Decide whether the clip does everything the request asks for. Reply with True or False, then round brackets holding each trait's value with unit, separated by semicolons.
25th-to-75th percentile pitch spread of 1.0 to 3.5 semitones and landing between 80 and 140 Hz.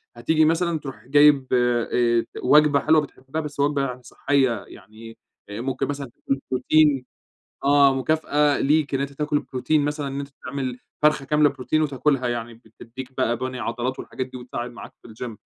True (3.1 semitones; 135 Hz)